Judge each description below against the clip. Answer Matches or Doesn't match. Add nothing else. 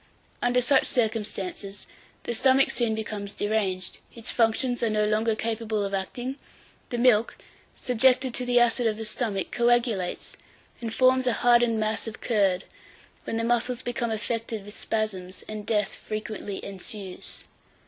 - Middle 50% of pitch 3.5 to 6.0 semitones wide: Doesn't match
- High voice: Matches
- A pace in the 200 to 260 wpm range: Doesn't match